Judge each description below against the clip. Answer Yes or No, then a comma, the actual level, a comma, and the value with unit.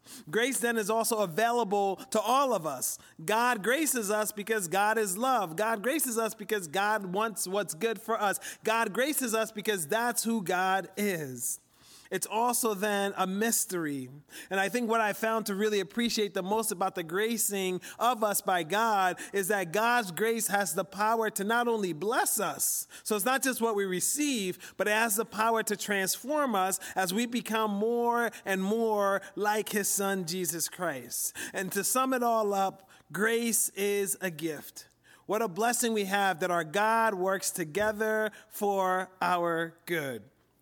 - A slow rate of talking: No, average, 175 wpm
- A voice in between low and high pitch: No, high, 210 Hz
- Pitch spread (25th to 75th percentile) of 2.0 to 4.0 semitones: Yes, average, 3.0 semitones